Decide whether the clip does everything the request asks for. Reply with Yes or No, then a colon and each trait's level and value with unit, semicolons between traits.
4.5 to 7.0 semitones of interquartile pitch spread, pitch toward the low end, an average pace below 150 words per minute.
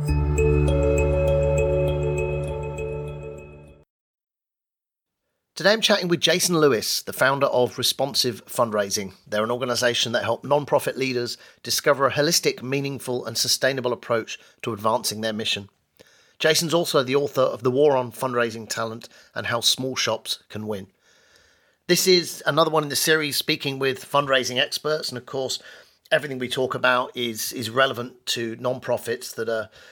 Yes: average, 4.9 semitones; low, 125 Hz; average, 140 wpm